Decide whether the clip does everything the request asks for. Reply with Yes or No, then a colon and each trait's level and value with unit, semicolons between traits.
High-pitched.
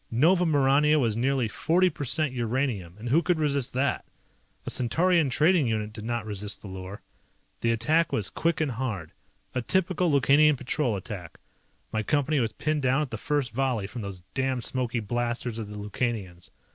No: low, 125 Hz